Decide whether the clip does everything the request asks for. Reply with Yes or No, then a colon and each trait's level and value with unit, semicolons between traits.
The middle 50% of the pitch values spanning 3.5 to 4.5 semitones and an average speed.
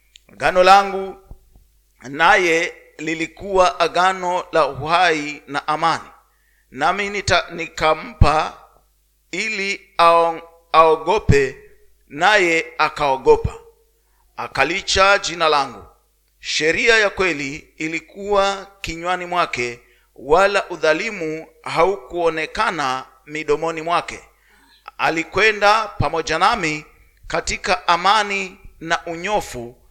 No: average, 4.0 semitones; slow, 70 wpm